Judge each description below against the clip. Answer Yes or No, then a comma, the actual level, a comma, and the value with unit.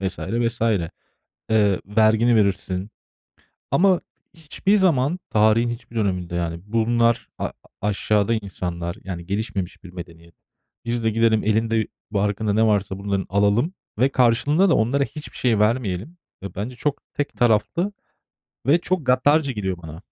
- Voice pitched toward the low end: Yes, low, 110 Hz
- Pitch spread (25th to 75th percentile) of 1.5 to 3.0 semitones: No, average, 4.1 semitones